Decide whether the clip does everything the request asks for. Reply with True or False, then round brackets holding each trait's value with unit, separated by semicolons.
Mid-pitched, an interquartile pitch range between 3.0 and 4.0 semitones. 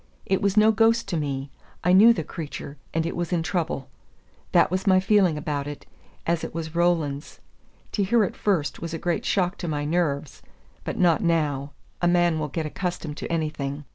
True (165 Hz; 3.7 semitones)